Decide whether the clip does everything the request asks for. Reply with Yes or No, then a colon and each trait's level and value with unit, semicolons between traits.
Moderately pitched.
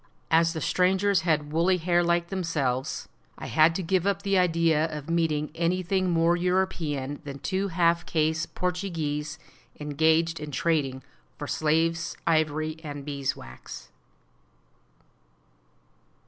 Yes: medium, 165 Hz